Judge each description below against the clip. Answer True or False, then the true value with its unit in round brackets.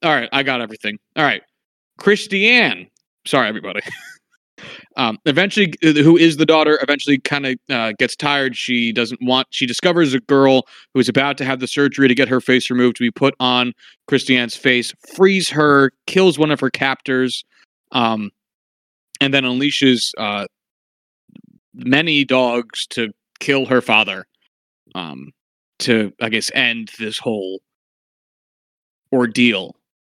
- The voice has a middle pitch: False (130 Hz)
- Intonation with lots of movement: False (3.2 semitones)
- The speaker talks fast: False (145 wpm)